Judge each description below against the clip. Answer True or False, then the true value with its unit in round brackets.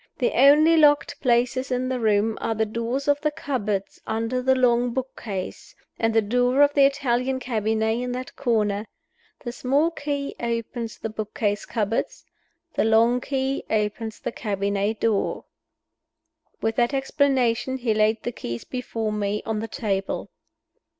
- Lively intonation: False (3.2 semitones)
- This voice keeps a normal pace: True (155 wpm)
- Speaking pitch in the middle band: False (235 Hz)